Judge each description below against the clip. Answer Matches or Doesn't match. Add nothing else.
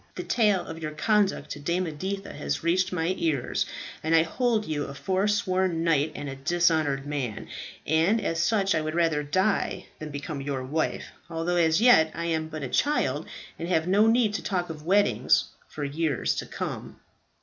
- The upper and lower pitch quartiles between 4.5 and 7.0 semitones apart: Doesn't match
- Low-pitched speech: Doesn't match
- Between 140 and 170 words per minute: Doesn't match